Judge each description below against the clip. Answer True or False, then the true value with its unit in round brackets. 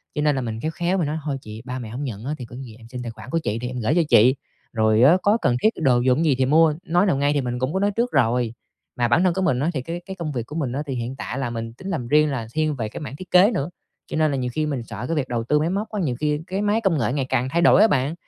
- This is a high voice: False (140 Hz)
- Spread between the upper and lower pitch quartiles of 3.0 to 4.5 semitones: False (5.2 semitones)